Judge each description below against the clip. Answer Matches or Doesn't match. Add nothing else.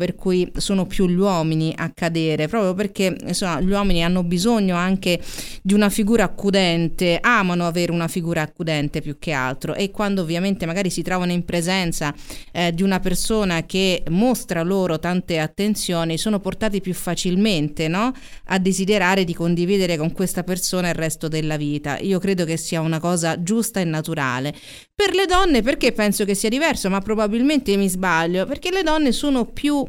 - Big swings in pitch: Doesn't match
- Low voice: Doesn't match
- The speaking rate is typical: Doesn't match